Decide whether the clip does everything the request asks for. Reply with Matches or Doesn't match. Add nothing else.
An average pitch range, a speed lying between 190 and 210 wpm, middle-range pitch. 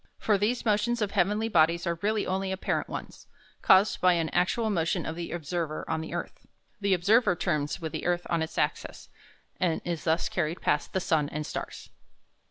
Matches